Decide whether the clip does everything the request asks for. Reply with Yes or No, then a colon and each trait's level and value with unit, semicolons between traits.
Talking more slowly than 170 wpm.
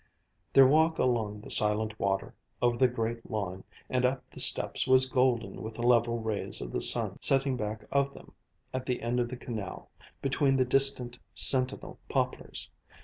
No: average, 175 wpm